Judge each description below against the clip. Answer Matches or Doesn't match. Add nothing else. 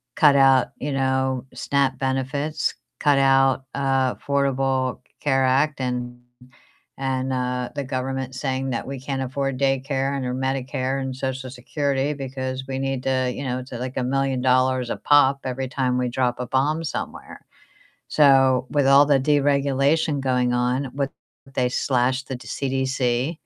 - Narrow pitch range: Matches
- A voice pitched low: Matches